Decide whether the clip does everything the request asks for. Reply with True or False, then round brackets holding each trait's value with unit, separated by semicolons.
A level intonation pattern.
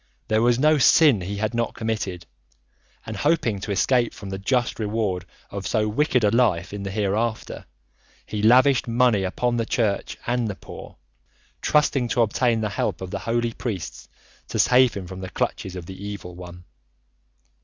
False (3.7 semitones)